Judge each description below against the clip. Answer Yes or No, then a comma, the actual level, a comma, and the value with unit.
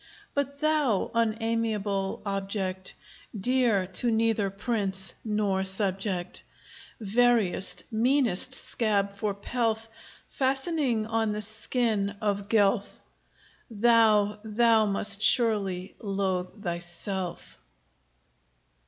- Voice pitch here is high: Yes, high, 210 Hz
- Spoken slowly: Yes, slow, 85 wpm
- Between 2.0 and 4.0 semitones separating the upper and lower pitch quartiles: Yes, average, 2.8 semitones